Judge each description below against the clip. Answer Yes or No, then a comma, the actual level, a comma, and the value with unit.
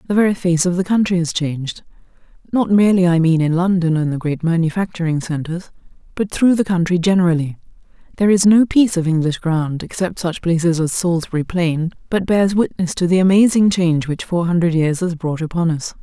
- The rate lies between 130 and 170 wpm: No, average, 195 wpm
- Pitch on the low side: No, medium, 175 Hz